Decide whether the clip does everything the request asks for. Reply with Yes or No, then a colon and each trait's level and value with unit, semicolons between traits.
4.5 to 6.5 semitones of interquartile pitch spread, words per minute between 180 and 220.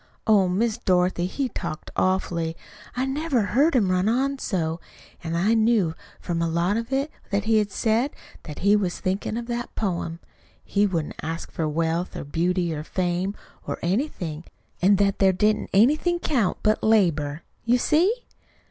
No: average, 5.1 semitones; average, 165 wpm